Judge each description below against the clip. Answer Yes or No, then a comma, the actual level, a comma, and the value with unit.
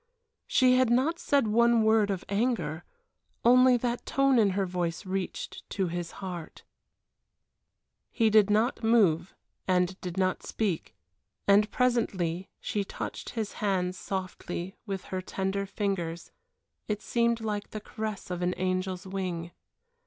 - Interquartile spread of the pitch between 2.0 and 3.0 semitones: No, average, 3.6 semitones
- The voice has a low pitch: No, high, 200 Hz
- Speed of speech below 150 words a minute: Yes, average, 140 wpm